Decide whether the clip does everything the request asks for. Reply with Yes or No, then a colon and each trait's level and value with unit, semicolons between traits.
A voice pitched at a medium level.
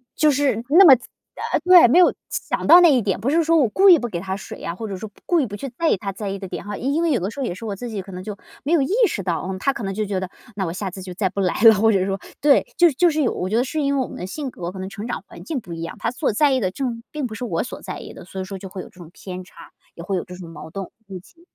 No: high, 210 Hz